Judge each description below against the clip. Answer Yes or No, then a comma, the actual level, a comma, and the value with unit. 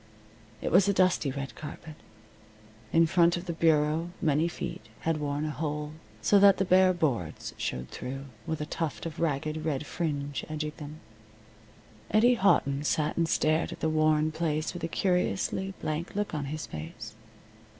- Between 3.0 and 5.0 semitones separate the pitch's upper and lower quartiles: No, narrow, 2.5 semitones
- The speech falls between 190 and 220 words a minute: No, average, 170 wpm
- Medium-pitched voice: Yes, medium, 155 Hz